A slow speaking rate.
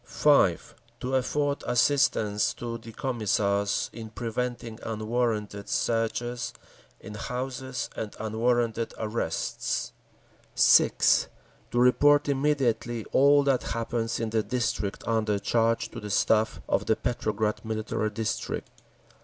Yes: slow, 110 wpm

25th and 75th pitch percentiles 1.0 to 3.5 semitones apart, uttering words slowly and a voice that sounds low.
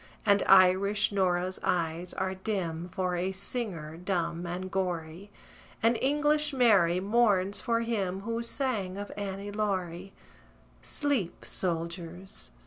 No: average, 3.1 semitones; slow, 120 wpm; high, 190 Hz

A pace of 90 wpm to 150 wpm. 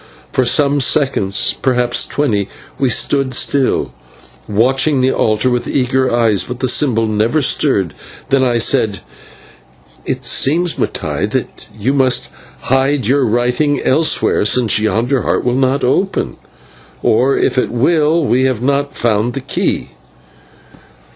Yes: average, 140 wpm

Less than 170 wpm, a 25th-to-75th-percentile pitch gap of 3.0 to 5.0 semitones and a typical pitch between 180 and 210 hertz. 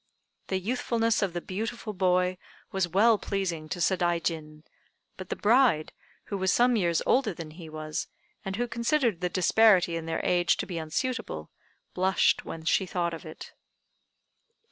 Yes: average, 160 wpm; average, 4.6 semitones; medium, 185 Hz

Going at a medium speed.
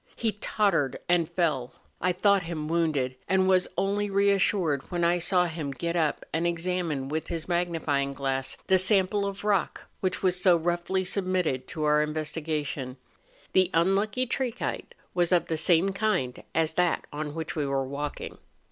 Yes: average, 170 wpm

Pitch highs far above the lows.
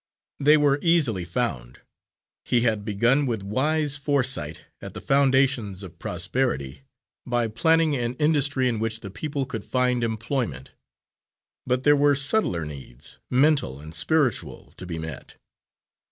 Yes: wide, 6.6 semitones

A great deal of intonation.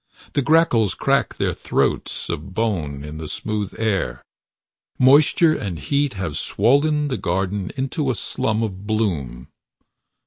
Yes: wide, 7.1 semitones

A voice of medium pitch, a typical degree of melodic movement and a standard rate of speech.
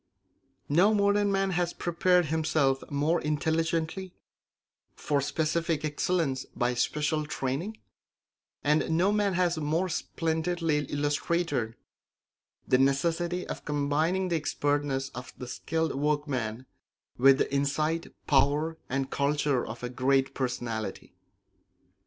No: medium, 150 Hz; average, 3.6 semitones; slow, 110 wpm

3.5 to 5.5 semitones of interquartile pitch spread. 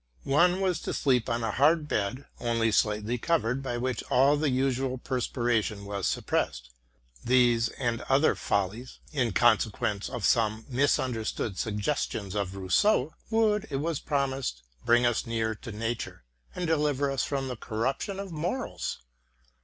Yes: average, 4.3 semitones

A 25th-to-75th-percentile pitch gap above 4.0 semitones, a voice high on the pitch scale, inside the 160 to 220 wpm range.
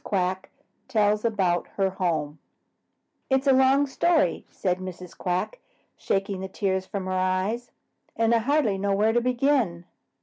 No: average, 4.4 semitones; high, 200 Hz; average, 145 wpm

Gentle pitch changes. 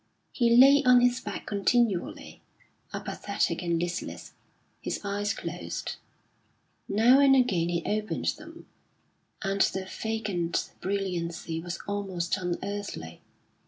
No: average, 4.4 semitones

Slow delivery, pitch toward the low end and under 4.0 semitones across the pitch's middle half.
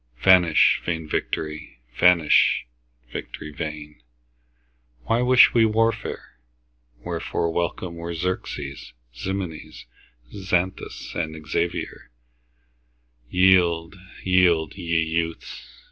Yes: slow, 80 wpm; very low, 85 Hz; narrow, 2.6 semitones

